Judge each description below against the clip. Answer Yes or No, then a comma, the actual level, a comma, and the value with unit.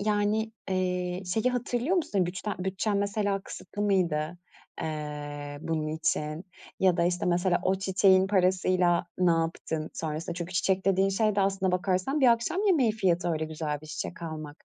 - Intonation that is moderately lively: Yes, average, 3.6 semitones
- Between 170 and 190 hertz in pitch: Yes, medium, 185 Hz